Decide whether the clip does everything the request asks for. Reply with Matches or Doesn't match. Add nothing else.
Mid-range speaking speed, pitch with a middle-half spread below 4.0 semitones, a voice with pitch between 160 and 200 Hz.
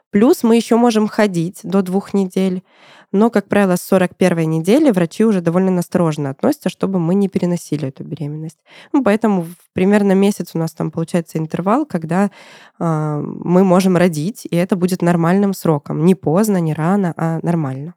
Doesn't match